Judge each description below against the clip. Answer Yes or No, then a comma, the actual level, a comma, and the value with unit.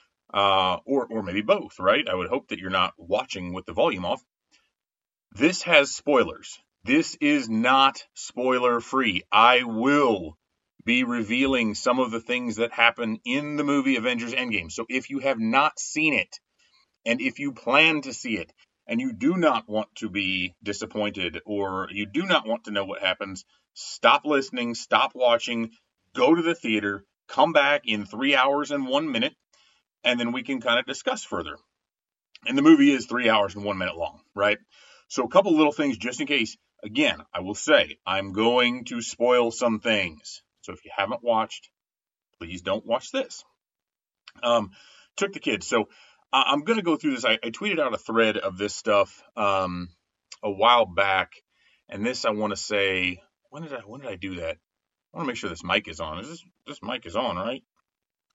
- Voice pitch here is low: Yes, low, 120 Hz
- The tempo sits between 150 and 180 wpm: No, average, 190 wpm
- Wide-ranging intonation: Yes, wide, 6.3 semitones